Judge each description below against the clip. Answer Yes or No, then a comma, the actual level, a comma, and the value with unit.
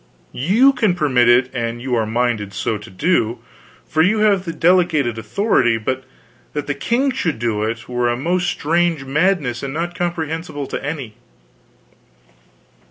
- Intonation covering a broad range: Yes, wide, 6.6 semitones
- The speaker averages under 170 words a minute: Yes, average, 160 wpm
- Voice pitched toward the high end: No, medium, 140 Hz